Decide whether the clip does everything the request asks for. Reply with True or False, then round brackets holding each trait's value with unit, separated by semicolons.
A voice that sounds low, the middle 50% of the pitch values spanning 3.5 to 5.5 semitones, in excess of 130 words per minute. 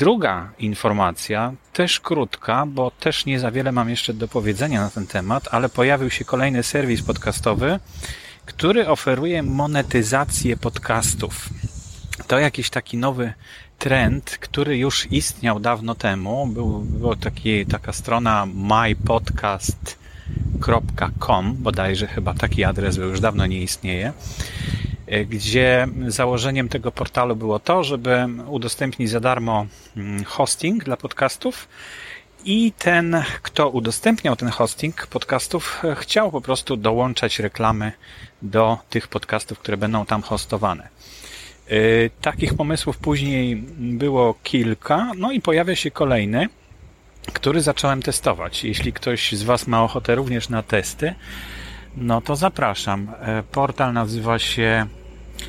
False (115 Hz; 4.0 semitones; 120 wpm)